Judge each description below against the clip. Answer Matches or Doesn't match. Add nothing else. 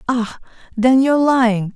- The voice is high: Matches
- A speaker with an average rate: Matches